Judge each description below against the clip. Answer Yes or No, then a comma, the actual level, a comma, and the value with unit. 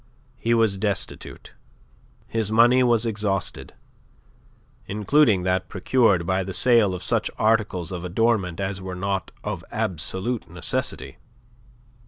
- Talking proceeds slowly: Yes, slow, 120 wpm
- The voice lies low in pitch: Yes, low, 100 Hz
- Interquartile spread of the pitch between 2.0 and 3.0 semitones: No, average, 3.5 semitones